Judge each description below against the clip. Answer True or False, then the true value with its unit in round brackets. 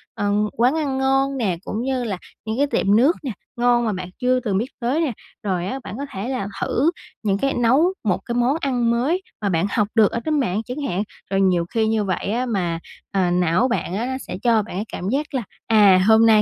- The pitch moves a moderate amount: True (4.7 semitones)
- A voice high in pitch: True (230 Hz)